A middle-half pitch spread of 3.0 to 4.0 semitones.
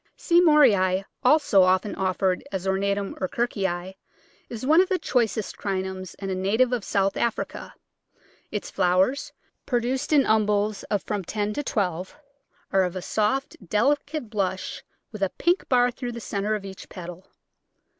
No: average, 4.5 semitones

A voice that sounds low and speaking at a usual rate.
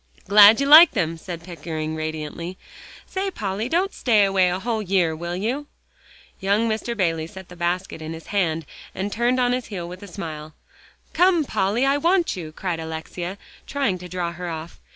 No: high, 190 Hz; average, 185 wpm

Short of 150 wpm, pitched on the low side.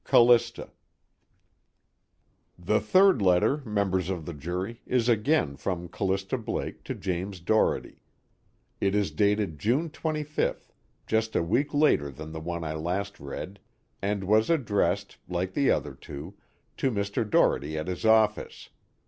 Yes: average, 140 wpm; low, 100 Hz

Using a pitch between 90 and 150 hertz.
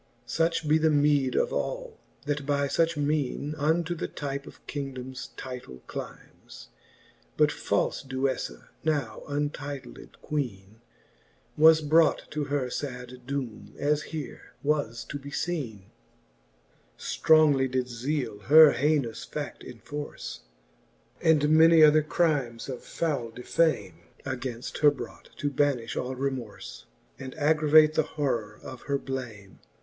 Yes: medium, 140 Hz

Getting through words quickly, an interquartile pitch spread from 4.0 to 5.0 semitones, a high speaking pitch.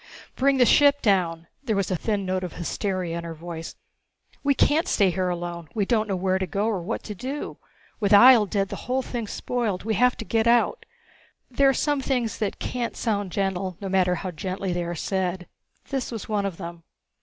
Yes: fast, 210 wpm; average, 4.6 semitones; high, 200 Hz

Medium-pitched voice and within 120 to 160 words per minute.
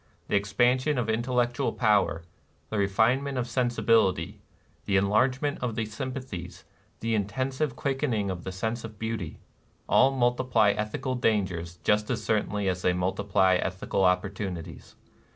No: low, 110 Hz; average, 145 wpm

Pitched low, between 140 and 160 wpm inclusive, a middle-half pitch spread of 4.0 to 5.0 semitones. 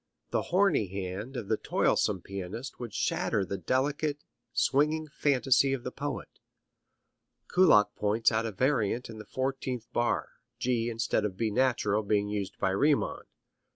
Yes: low, 115 Hz; average, 150 wpm; average, 4.6 semitones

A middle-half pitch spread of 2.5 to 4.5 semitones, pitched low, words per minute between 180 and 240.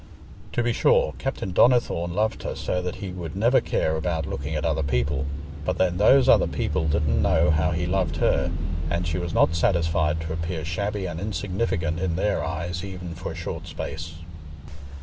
Yes: average, 2.8 semitones; very low, 85 Hz; average, 190 wpm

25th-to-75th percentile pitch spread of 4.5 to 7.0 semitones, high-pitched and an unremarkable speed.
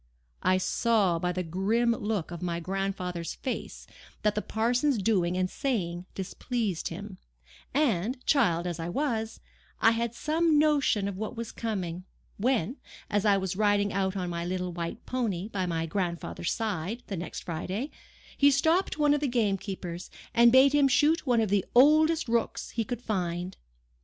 Yes: average, 5.2 semitones; high, 205 Hz; average, 165 wpm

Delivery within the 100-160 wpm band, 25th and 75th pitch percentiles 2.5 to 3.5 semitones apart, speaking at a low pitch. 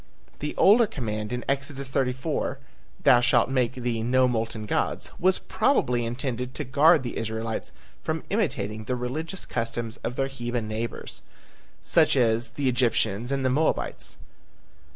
Yes: average, 145 wpm; average, 3.2 semitones; low, 125 Hz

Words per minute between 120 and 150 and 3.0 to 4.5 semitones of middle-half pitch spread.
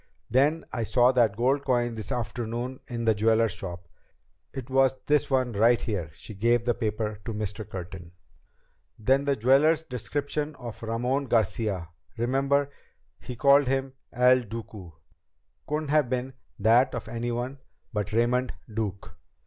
Yes: average, 145 wpm; average, 3.4 semitones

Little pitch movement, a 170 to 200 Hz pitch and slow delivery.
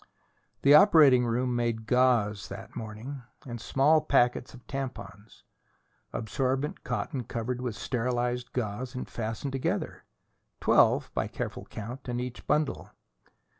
No: narrow, 2.3 semitones; low, 125 Hz; slow, 125 wpm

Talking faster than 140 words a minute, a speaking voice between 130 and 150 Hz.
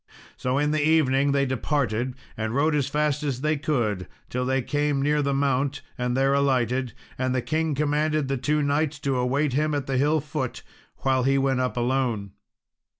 Yes: average, 190 wpm; low, 135 Hz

